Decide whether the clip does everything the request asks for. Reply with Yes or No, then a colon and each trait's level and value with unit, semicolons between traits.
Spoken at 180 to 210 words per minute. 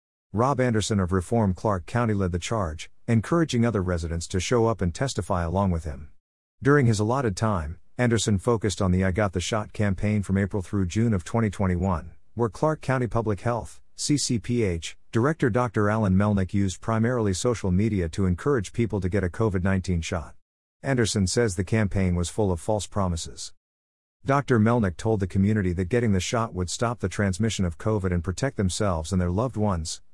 Yes: average, 185 wpm